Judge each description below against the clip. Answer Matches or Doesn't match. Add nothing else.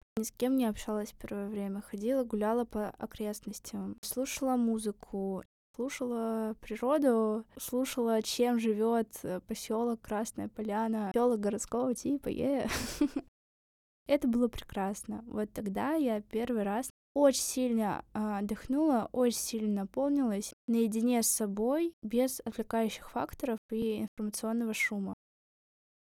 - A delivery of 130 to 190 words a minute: Doesn't match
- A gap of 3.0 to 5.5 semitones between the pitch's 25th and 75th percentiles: Doesn't match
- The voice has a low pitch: Doesn't match